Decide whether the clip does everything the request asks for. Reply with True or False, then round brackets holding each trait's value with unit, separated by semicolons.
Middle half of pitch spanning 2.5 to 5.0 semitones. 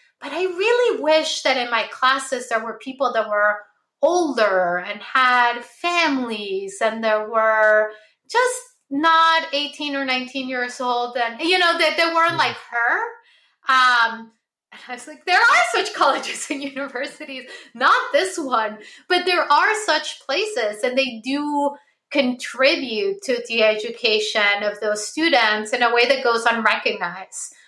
False (5.6 semitones)